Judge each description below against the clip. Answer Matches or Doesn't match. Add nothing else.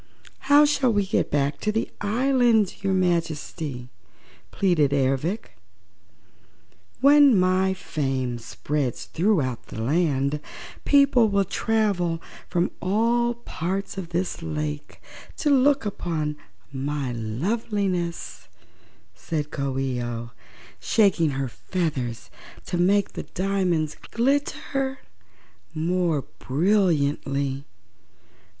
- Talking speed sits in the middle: Doesn't match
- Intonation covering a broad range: Matches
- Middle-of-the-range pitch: Matches